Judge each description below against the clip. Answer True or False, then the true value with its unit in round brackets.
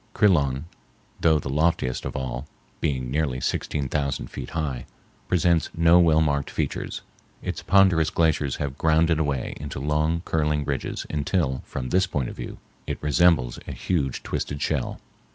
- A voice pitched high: False (75 Hz)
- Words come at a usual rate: True (155 wpm)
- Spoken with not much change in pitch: False (3.3 semitones)